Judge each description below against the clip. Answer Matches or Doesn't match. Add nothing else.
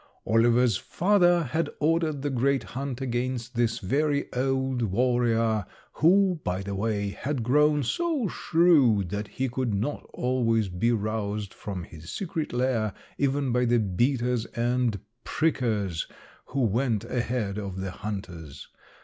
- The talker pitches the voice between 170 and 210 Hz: Doesn't match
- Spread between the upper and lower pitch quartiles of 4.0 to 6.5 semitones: Matches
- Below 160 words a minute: Matches